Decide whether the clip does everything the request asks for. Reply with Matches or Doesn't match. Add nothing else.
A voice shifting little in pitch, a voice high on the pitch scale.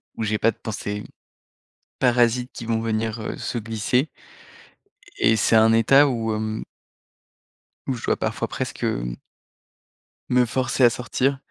Doesn't match